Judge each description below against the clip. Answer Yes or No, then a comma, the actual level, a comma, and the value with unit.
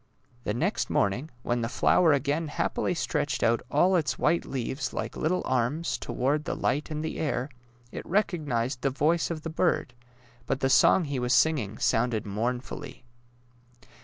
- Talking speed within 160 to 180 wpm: Yes, average, 165 wpm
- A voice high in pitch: No, medium, 140 Hz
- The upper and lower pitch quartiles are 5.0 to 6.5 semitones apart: No, average, 4.4 semitones